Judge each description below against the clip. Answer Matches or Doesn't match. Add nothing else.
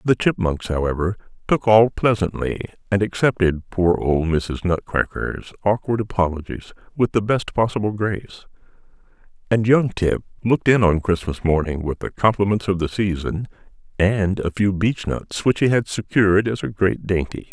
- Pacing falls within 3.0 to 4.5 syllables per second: Doesn't match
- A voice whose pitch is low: Matches